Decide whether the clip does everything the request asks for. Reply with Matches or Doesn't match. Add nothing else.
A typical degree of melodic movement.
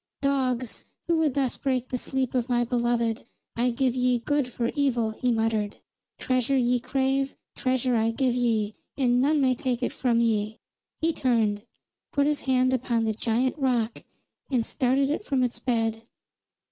Doesn't match